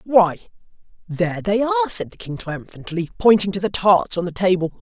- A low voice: No, high, 190 Hz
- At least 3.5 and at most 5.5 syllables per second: Yes, 5.4 syllables/s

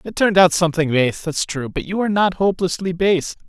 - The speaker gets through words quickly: Yes, fast, 225 wpm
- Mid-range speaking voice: Yes, medium, 175 Hz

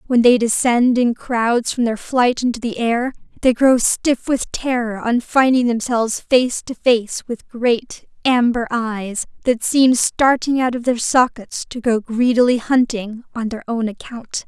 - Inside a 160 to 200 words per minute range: Yes, average, 170 wpm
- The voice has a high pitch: Yes, high, 240 Hz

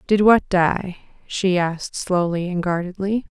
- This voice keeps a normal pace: Yes, average, 145 wpm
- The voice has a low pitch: No, medium, 185 Hz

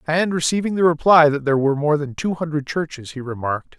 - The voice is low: No, medium, 155 Hz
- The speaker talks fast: Yes, fast, 220 wpm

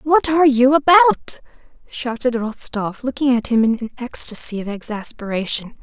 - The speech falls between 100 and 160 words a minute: Yes, average, 145 wpm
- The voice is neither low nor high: No, very high, 250 Hz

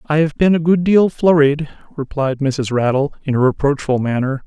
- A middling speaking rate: Yes, average, 190 wpm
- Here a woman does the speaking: No, male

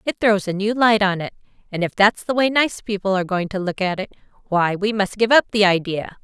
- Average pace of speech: No, fast, 260 wpm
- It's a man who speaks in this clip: No, female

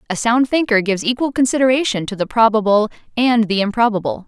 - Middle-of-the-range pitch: No, high, 225 Hz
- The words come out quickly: No, average, 170 wpm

